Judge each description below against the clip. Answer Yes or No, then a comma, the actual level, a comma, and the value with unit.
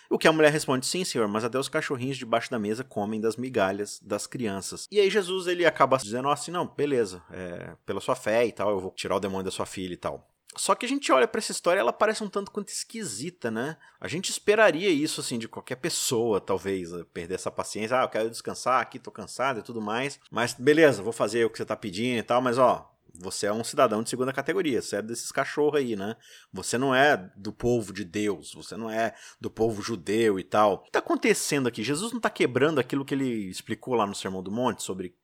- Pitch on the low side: Yes, low, 125 Hz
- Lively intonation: Yes, wide, 7.7 semitones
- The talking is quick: Yes, fast, 240 wpm